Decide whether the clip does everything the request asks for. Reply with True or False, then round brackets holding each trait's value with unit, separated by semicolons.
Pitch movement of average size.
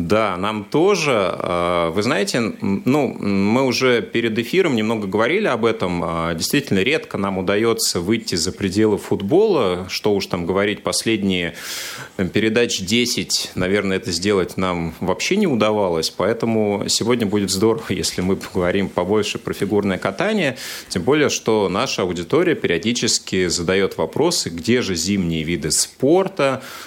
True (3.5 semitones)